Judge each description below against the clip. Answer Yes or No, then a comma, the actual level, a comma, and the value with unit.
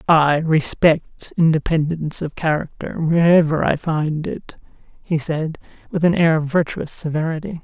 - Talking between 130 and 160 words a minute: Yes, slow, 135 wpm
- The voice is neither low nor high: Yes, medium, 160 Hz